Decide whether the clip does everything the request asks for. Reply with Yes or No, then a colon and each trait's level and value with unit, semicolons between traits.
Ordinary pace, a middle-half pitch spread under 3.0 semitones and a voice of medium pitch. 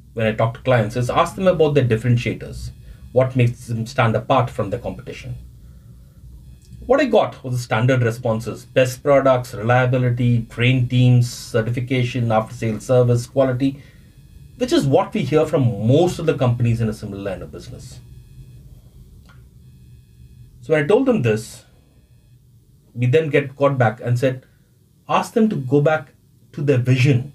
No: average, 160 wpm; narrow, 2.5 semitones; low, 125 Hz